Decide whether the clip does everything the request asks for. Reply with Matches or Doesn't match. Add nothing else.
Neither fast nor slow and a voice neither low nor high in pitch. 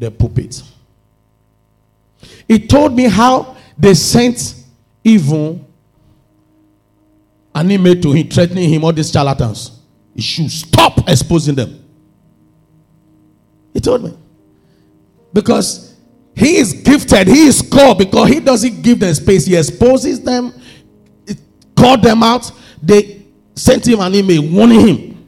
Doesn't match